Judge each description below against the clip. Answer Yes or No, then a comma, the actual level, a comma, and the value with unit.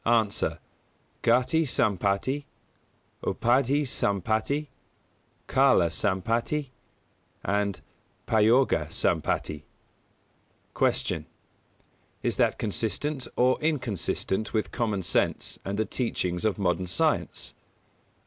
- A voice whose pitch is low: Yes, low, 110 Hz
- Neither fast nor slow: No, slow, 90 wpm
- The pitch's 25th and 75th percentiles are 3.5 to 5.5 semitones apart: Yes, average, 4.6 semitones